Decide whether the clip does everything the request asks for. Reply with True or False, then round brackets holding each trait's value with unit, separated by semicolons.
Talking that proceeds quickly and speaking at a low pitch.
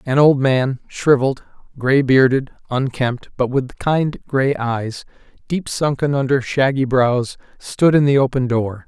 False (150 wpm; 130 Hz)